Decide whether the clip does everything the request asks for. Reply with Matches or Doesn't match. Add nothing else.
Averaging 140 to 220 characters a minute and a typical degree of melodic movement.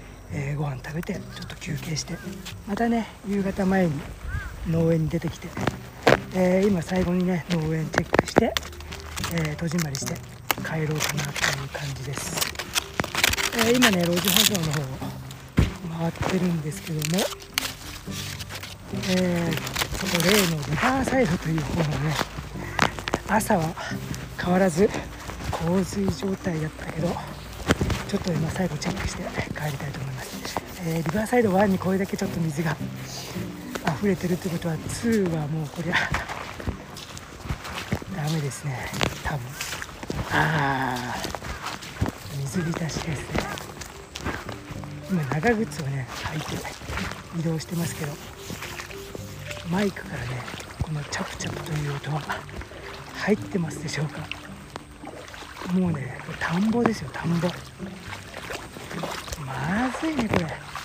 Doesn't match